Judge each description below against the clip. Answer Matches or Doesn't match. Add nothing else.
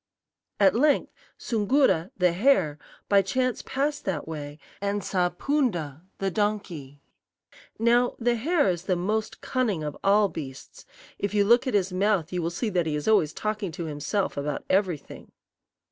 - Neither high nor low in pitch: Doesn't match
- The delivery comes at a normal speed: Matches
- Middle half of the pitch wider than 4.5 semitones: Matches